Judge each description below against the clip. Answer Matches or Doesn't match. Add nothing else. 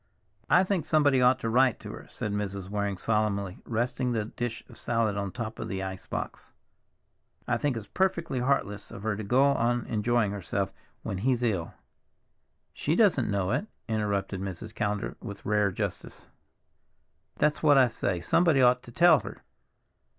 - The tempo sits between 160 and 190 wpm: Matches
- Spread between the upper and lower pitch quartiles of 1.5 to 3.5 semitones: Doesn't match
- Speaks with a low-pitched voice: Matches